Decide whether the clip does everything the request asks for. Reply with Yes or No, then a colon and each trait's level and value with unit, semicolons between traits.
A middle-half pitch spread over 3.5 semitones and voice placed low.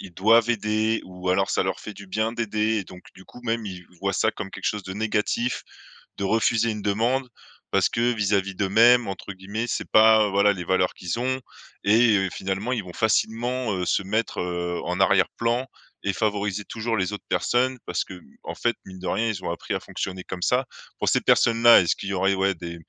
No: average, 3.1 semitones; low, 105 Hz